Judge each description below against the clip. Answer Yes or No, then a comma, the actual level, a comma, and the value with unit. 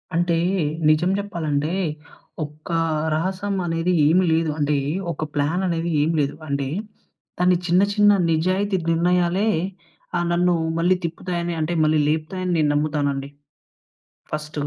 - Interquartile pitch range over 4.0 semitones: No, average, 2.8 semitones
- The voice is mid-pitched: Yes, medium, 165 Hz